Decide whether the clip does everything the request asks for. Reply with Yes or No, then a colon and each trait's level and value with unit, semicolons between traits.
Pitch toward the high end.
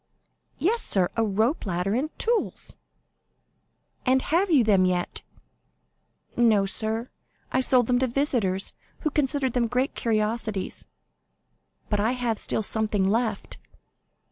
Yes: high, 230 Hz